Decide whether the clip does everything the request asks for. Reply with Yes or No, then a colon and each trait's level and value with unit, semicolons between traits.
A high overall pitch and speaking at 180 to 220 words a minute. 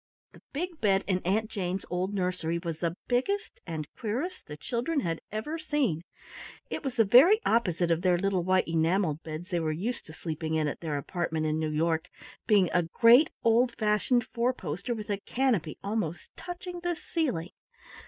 Yes: high, 195 Hz; average, 185 wpm